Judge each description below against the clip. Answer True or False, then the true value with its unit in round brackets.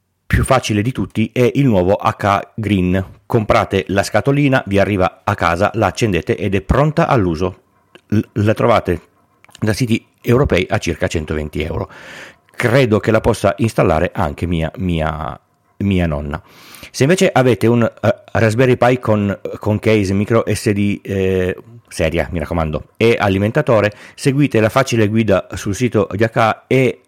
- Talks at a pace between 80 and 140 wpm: False (150 wpm)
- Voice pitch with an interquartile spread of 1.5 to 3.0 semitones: False (3.8 semitones)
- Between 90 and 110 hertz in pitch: True (105 Hz)